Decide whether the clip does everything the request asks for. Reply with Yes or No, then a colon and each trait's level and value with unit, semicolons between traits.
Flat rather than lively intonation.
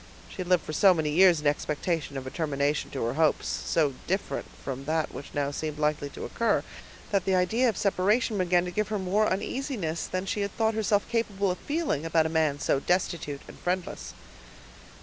No: average, 5.0 semitones